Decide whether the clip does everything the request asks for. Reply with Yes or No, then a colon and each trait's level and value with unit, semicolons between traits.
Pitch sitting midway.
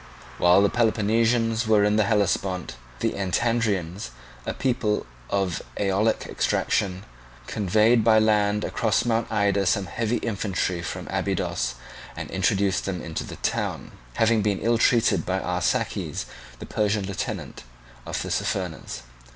No: low, 105 Hz